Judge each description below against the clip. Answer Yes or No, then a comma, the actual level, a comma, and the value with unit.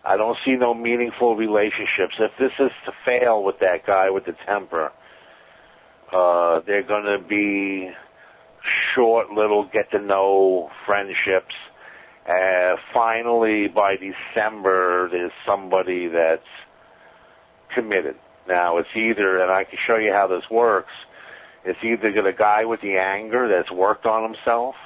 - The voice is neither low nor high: No, low, 100 Hz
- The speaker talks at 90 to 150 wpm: Yes, average, 140 wpm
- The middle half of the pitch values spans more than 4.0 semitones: No, average, 3.2 semitones